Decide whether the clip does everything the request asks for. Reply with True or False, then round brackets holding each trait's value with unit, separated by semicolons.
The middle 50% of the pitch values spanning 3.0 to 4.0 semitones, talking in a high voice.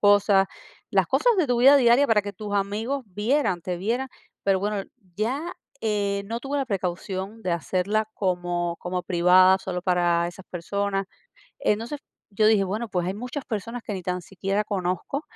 True (3.7 semitones; 200 Hz)